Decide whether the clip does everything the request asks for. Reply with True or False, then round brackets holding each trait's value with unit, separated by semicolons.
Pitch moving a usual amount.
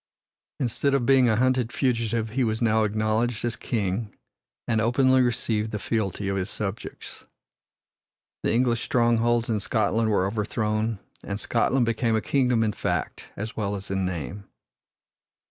False (2.2 semitones)